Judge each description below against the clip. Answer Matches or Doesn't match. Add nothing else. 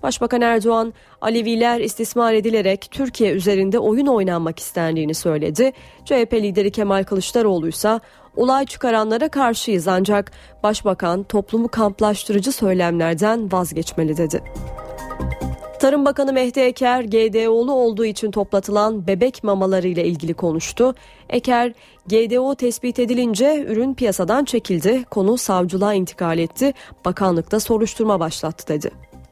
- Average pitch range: Matches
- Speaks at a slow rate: Doesn't match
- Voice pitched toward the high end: Matches